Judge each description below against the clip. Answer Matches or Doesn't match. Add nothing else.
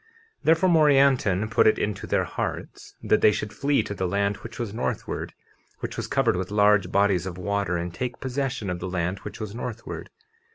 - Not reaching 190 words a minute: Doesn't match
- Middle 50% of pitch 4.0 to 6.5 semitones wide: Matches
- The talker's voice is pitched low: Matches